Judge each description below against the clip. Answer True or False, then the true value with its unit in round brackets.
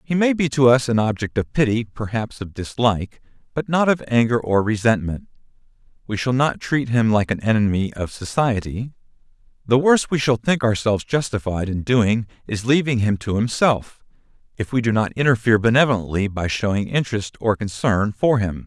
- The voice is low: True (115 Hz)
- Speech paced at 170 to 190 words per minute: True (175 wpm)